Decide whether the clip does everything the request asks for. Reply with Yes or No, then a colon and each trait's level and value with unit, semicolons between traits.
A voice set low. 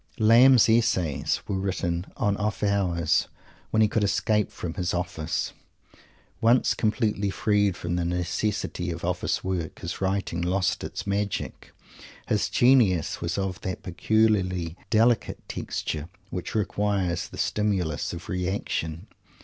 Yes: very low, 95 Hz